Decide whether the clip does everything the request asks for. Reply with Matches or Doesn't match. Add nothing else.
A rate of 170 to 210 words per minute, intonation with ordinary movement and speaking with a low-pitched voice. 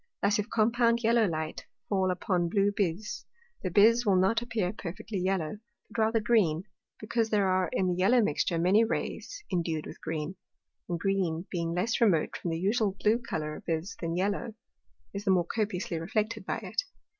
Doesn't match